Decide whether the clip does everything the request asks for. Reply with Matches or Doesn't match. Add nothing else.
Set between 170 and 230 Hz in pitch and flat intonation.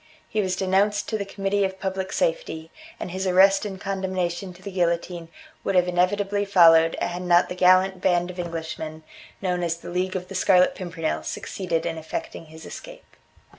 Matches